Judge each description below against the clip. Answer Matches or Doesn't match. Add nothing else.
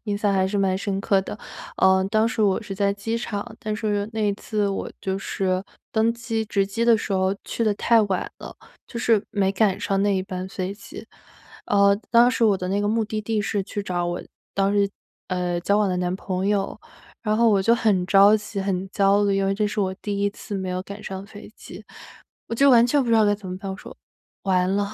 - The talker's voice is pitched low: Doesn't match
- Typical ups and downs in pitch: Doesn't match